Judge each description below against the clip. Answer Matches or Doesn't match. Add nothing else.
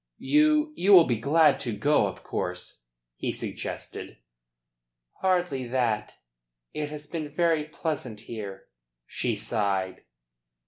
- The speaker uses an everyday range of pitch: Doesn't match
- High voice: Doesn't match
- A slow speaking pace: Matches